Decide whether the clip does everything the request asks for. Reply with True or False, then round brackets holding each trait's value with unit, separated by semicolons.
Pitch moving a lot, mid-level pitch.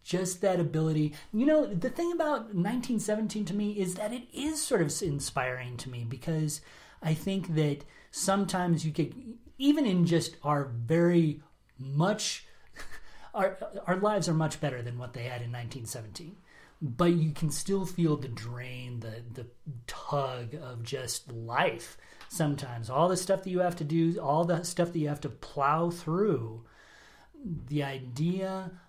True (5.7 semitones; 165 Hz)